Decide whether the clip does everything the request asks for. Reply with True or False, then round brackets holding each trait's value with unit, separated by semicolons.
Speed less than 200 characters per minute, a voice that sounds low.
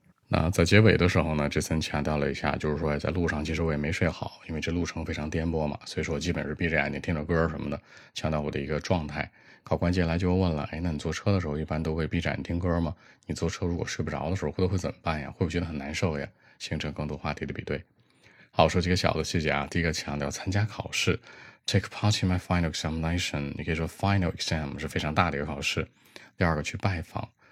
False (435 characters per minute; 80 Hz)